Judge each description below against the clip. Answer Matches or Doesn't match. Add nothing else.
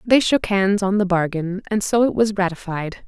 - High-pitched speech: Matches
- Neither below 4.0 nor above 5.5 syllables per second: Matches